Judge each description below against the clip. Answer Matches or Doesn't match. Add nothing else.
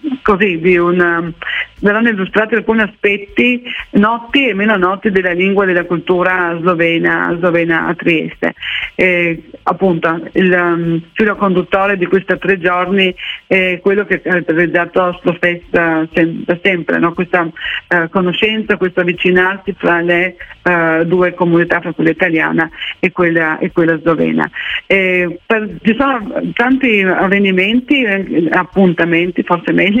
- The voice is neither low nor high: Matches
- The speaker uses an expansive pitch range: Doesn't match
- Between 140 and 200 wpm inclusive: Doesn't match